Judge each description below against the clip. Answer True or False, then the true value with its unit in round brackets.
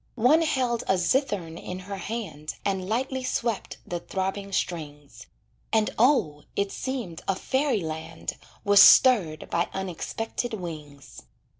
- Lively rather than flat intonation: True (6.2 semitones)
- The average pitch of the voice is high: True (195 Hz)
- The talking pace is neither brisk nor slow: False (130 wpm)